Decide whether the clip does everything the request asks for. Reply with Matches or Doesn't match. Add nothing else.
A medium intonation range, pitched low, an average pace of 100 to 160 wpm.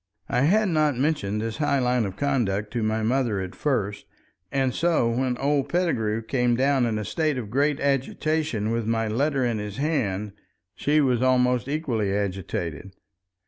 Doesn't match